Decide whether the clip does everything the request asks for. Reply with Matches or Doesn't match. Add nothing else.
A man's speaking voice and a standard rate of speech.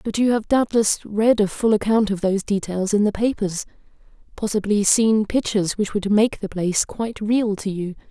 Doesn't match